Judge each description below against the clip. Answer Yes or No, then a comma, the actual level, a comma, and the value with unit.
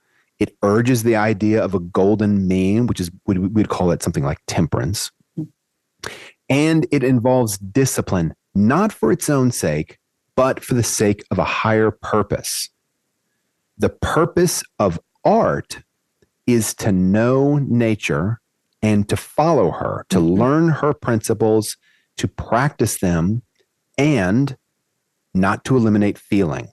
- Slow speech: Yes, slow, 130 wpm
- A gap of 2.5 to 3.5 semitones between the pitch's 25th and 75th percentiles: No, average, 4.2 semitones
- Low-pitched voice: Yes, low, 110 Hz